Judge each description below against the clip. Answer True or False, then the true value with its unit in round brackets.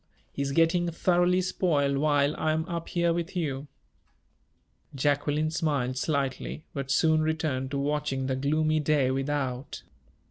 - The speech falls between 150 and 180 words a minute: False (140 wpm)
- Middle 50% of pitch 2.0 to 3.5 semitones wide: True (2.6 semitones)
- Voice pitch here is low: False (150 Hz)